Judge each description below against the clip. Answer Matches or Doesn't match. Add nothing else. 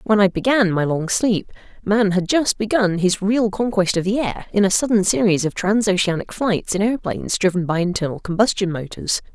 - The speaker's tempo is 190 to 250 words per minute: Matches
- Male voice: Doesn't match